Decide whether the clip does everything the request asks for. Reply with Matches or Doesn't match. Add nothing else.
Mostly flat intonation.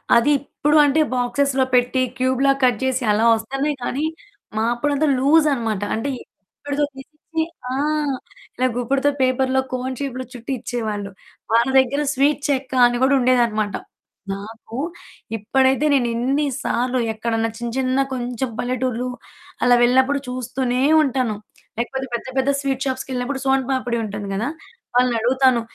Matches